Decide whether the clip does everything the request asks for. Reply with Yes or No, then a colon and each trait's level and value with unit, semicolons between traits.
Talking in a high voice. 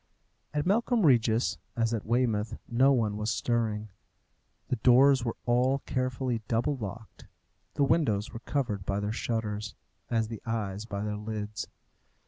No: low, 115 Hz